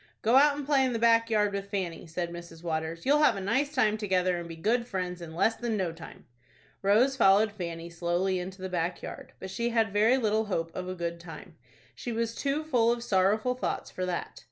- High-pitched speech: Yes, high, 200 Hz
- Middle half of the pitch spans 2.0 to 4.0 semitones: No, average, 4.9 semitones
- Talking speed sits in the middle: No, fast, 225 wpm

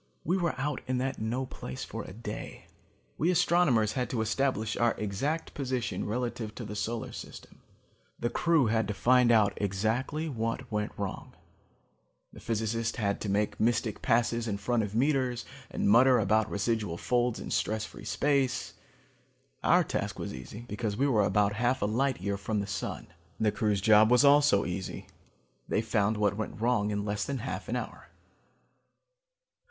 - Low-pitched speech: Yes, low, 115 Hz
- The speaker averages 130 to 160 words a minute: No, average, 170 wpm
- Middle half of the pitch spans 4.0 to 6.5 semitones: No, average, 3.3 semitones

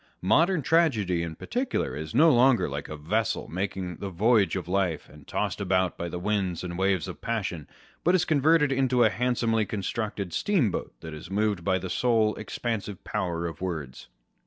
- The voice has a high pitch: No, low, 100 Hz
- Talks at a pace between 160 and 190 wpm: Yes, average, 180 wpm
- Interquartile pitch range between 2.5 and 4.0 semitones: No, wide, 5.5 semitones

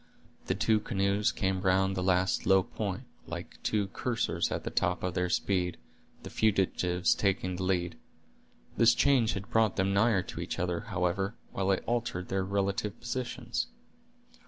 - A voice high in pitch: No, very low, 95 Hz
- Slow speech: No, average, 160 wpm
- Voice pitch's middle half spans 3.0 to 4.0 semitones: No, narrow, 2.5 semitones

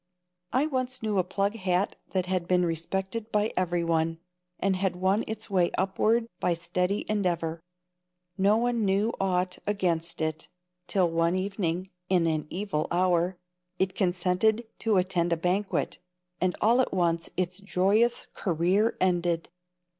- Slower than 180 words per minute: Yes, average, 145 wpm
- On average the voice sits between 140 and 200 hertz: Yes, medium, 185 Hz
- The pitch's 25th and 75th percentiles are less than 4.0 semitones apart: Yes, average, 2.9 semitones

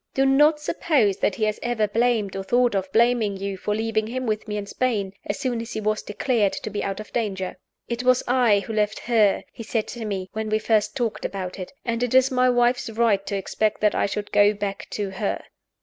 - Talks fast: Yes, fast, 235 wpm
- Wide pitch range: No, average, 3.0 semitones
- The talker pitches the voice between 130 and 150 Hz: No, high, 215 Hz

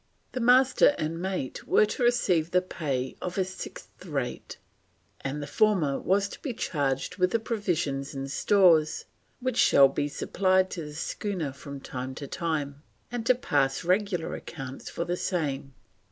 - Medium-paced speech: Yes, average, 165 wpm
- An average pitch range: No, wide, 6.0 semitones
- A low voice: No, medium, 170 Hz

